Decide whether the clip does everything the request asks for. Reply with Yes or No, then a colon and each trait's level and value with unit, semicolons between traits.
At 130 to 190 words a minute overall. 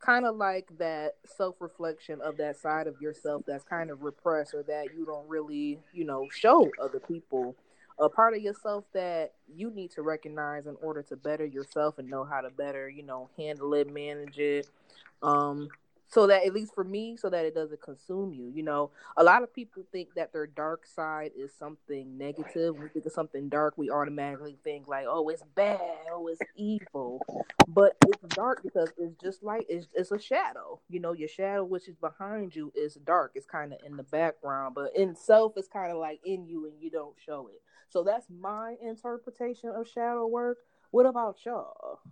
No: fast, 205 wpm